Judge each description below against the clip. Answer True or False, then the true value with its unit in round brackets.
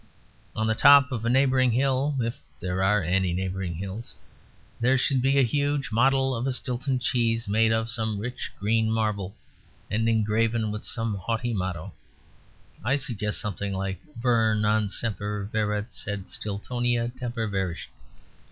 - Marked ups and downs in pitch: False (3.3 semitones)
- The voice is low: True (110 Hz)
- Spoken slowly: False (150 wpm)